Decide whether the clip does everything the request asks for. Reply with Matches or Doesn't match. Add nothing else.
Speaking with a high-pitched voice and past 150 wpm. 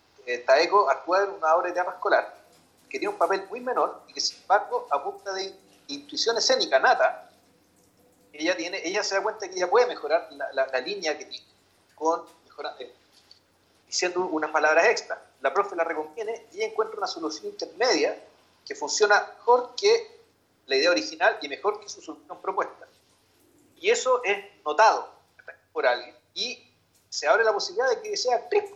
Matches